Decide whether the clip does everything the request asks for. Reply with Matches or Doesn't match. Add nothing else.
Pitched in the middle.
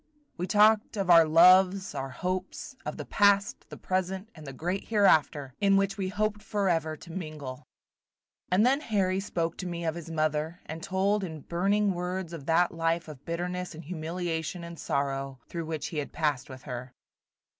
Matches